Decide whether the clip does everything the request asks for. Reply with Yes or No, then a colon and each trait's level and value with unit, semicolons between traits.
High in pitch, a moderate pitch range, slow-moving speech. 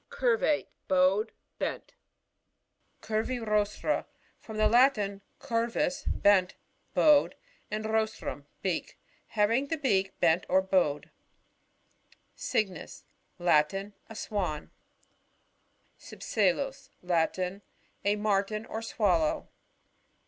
Yes: high, 210 Hz; average, 3.3 semitones; slow, 105 wpm